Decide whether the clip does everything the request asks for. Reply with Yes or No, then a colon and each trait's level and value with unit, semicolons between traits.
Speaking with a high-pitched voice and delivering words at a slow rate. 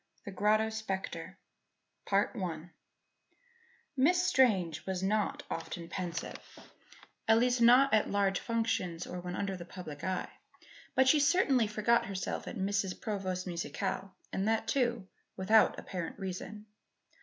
Yes: high, 200 Hz; slow, 125 wpm